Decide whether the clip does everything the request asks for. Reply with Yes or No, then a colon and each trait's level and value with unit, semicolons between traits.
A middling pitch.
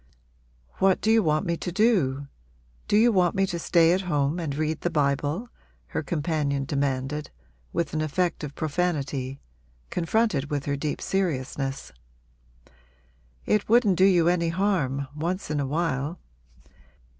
Yes: medium, 160 Hz